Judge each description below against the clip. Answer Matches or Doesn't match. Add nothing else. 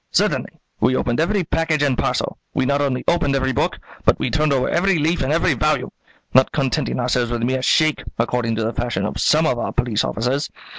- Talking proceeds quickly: Matches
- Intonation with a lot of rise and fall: Doesn't match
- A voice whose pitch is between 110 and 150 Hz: Matches